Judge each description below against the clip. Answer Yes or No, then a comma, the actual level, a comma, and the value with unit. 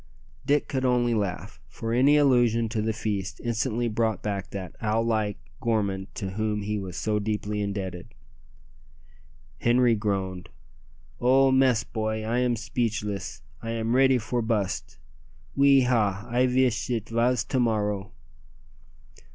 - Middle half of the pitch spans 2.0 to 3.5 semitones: Yes, average, 2.9 semitones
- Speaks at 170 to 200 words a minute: No, average, 140 wpm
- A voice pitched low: Yes, low, 110 Hz